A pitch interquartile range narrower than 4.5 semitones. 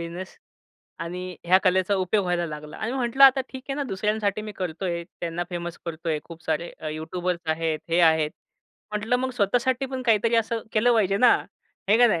No: average, 5.1 semitones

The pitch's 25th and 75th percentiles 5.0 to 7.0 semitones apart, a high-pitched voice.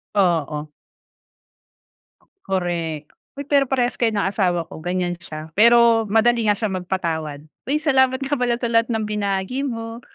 Yes: average, 5.3 semitones; high, 210 Hz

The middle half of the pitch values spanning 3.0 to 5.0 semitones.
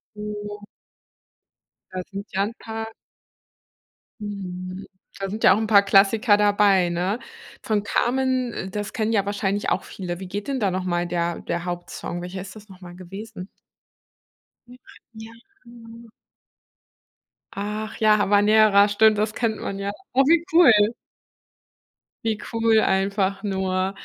No: narrow, 2.4 semitones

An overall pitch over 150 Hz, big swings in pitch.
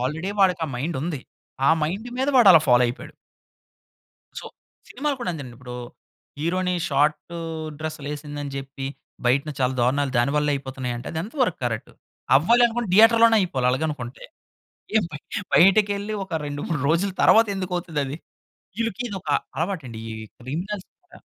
Yes: medium, 160 Hz; wide, 6.3 semitones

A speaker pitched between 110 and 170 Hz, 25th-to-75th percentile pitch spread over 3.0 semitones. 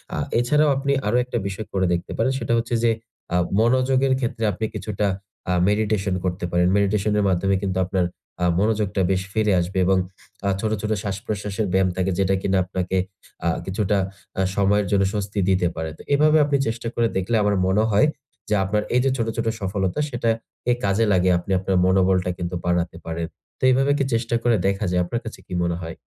No: low, 100 Hz; average, 3.4 semitones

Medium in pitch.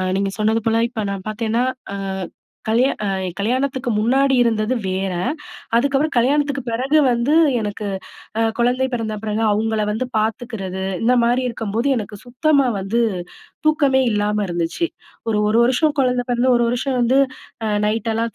No: high, 235 Hz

